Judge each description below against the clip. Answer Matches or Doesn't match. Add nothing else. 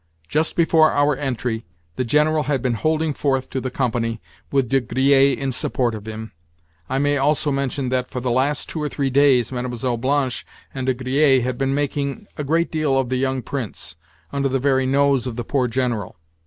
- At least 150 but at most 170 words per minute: Doesn't match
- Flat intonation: Matches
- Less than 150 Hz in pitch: Matches